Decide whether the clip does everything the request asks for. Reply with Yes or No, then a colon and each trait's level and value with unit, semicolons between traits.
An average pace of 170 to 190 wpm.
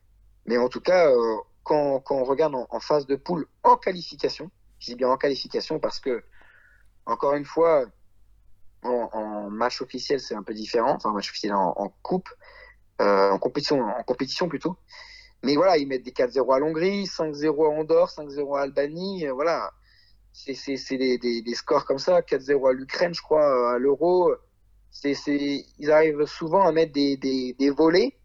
Yes: average, 185 wpm